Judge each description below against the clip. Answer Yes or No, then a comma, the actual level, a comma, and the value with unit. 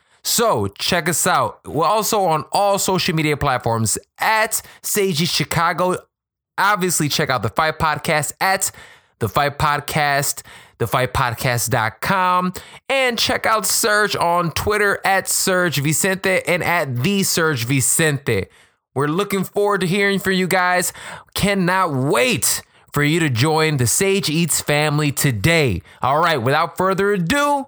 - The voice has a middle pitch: Yes, medium, 170 Hz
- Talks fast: No, average, 140 wpm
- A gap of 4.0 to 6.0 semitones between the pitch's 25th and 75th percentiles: Yes, average, 4.9 semitones